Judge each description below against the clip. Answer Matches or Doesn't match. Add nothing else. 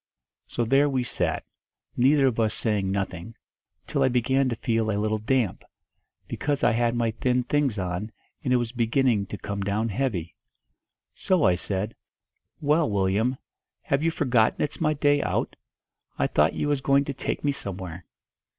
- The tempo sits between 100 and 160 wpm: Doesn't match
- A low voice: Matches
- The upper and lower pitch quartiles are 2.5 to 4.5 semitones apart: Doesn't match